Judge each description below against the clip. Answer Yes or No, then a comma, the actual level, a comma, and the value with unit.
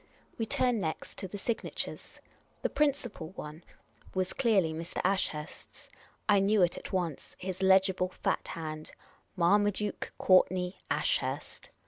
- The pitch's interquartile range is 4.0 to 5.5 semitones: No, average, 3.3 semitones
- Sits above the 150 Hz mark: Yes, high, 190 Hz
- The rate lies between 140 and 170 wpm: Yes, average, 145 wpm